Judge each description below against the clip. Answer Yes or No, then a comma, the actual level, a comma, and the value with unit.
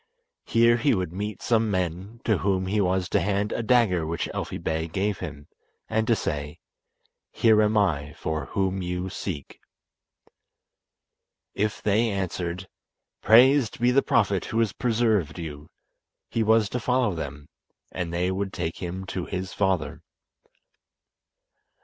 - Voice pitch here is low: Yes, very low, 95 Hz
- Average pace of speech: Yes, average, 145 wpm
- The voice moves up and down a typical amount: Yes, average, 4.0 semitones